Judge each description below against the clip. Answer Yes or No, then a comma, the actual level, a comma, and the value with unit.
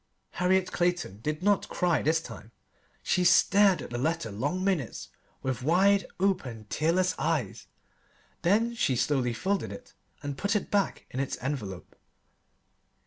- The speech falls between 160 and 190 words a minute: No, average, 140 wpm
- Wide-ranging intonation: Yes, wide, 6.4 semitones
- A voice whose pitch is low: No, medium, 165 Hz